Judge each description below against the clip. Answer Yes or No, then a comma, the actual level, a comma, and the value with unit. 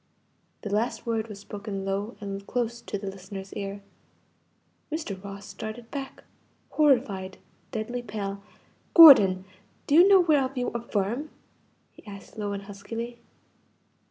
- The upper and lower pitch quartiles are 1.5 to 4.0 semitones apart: Yes, average, 3.5 semitones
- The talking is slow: Yes, slow, 130 wpm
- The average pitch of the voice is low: No, high, 215 Hz